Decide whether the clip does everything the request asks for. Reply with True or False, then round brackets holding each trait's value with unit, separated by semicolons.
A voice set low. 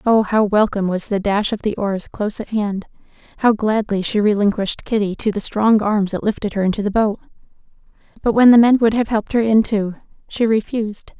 False (210 Hz)